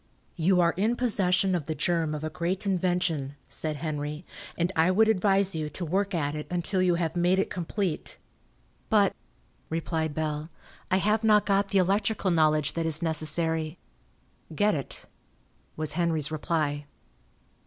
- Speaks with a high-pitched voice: No, medium, 170 Hz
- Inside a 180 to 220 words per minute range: No, average, 155 wpm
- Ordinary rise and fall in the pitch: Yes, average, 3.6 semitones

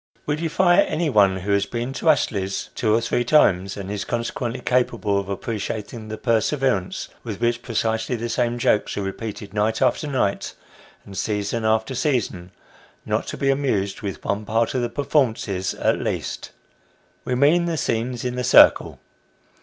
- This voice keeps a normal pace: Yes, average, 165 wpm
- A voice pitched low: Yes, low, 115 Hz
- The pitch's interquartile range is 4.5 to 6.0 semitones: No, average, 3.9 semitones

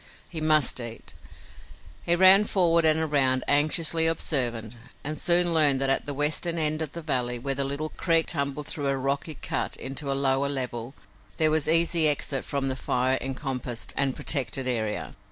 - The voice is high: No, medium, 140 Hz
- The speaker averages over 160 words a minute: Yes, average, 175 wpm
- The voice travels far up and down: No, average, 3.1 semitones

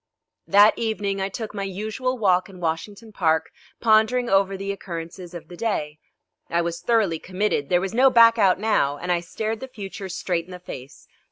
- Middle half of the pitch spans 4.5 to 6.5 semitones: No, average, 3.9 semitones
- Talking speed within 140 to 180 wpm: No, average, 190 wpm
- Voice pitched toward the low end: No, high, 195 Hz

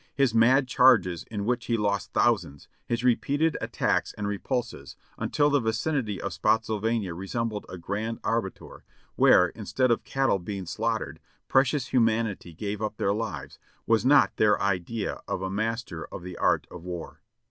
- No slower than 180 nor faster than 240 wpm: No, average, 160 wpm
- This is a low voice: Yes, low, 110 Hz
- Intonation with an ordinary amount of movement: Yes, average, 3.5 semitones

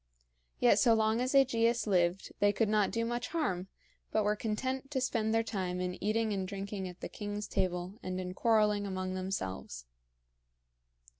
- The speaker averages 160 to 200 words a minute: Yes, average, 170 wpm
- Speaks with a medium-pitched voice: No, high, 205 Hz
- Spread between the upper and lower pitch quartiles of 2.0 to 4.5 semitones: Yes, average, 3.4 semitones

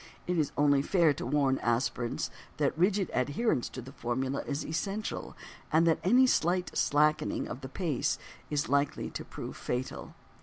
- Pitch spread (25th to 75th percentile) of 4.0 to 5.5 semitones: Yes, average, 4.7 semitones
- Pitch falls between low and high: Yes, medium, 145 Hz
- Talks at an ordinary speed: Yes, average, 160 wpm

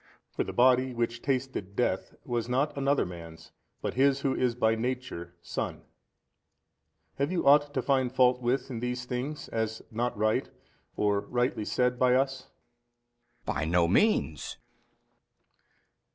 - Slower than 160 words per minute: Yes, average, 145 wpm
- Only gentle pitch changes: No, average, 3.0 semitones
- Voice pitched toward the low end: Yes, low, 125 Hz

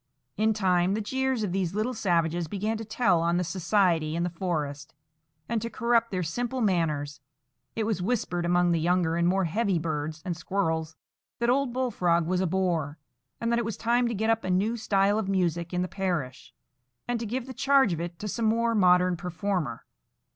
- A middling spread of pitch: Yes, average, 4.7 semitones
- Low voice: No, medium, 185 Hz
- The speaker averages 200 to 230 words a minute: Yes, fast, 205 wpm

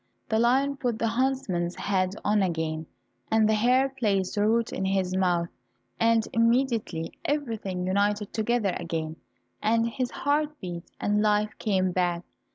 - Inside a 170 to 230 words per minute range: No, average, 150 wpm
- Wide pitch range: No, average, 4.0 semitones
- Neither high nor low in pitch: No, high, 210 Hz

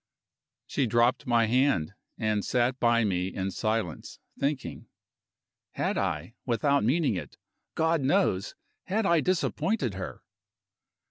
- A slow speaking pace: Yes, slow, 120 wpm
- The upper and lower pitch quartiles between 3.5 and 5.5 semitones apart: Yes, average, 5.2 semitones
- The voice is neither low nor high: No, low, 120 Hz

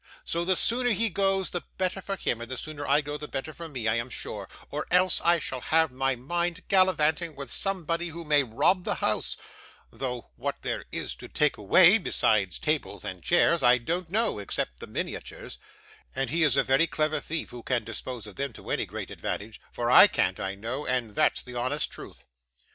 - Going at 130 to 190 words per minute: No, fast, 205 wpm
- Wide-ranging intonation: Yes, wide, 5.9 semitones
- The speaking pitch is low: No, medium, 150 Hz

